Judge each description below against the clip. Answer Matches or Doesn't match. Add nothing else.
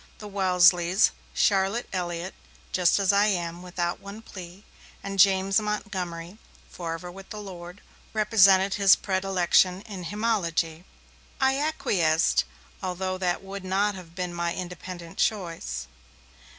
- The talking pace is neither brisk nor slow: Doesn't match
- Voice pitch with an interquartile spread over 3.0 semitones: Doesn't match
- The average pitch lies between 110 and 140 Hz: Doesn't match